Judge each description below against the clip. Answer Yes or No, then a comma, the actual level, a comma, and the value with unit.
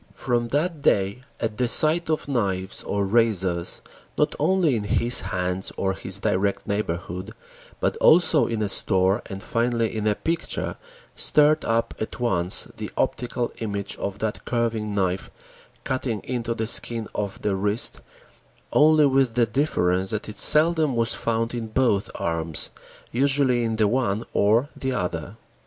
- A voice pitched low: Yes, low, 110 Hz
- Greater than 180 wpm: No, average, 155 wpm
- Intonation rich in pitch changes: No, average, 4.2 semitones